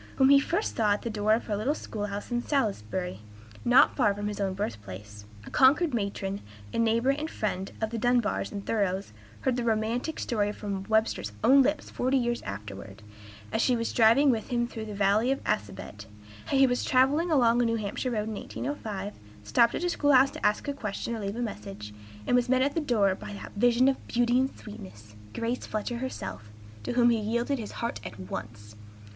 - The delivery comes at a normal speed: No, fast, 210 wpm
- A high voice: Yes, high, 225 Hz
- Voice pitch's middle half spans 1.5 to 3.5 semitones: No, average, 4.1 semitones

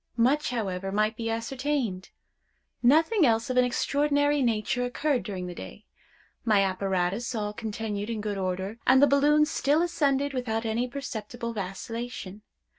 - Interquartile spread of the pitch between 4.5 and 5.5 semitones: Yes, average, 4.9 semitones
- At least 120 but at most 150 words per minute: Yes, average, 145 wpm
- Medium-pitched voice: No, high, 230 Hz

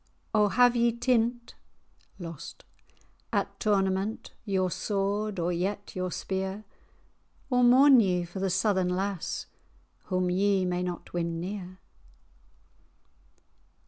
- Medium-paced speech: No, slow, 110 wpm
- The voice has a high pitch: Yes, high, 195 Hz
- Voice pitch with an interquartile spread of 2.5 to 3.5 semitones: Yes, average, 2.8 semitones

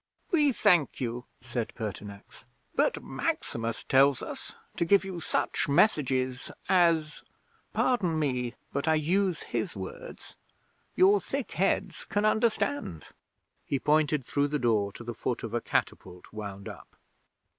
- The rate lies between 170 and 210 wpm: No, slow, 135 wpm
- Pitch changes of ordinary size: No, wide, 7.3 semitones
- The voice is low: No, medium, 145 Hz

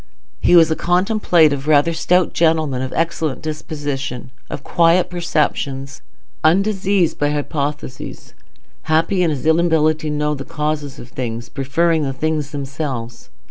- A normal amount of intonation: Yes, average, 3.1 semitones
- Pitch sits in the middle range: Yes, medium, 155 Hz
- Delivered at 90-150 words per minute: Yes, slow, 135 wpm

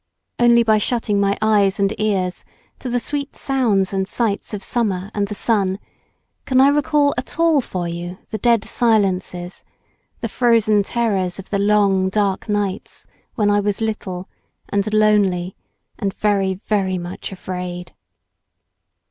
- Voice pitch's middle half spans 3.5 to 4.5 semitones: No, average, 3.0 semitones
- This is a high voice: Yes, high, 205 Hz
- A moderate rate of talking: Yes, average, 150 wpm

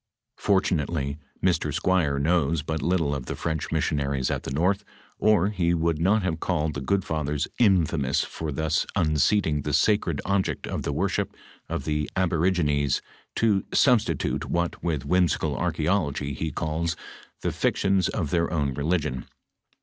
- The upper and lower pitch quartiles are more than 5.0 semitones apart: No, average, 3.7 semitones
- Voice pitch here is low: Yes, very low, 80 Hz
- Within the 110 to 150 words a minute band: Yes, average, 145 wpm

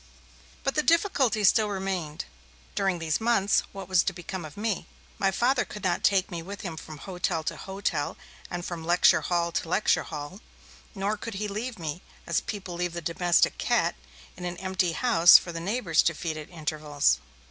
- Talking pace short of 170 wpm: No, average, 190 wpm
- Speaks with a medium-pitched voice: Yes, medium, 180 Hz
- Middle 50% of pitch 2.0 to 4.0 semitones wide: Yes, average, 3.4 semitones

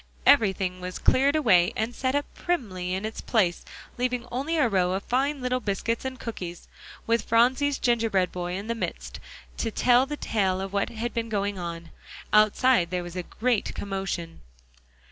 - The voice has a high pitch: Yes, high, 220 Hz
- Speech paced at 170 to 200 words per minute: Yes, average, 175 wpm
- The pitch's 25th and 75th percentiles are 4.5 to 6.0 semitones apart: Yes, average, 5.3 semitones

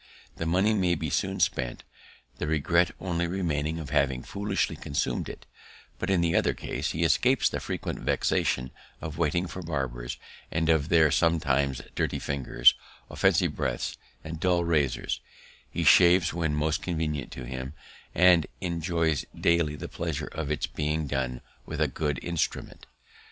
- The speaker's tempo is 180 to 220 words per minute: No, average, 155 wpm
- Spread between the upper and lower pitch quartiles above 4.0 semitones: No, average, 3.2 semitones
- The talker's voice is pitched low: Yes, very low, 80 Hz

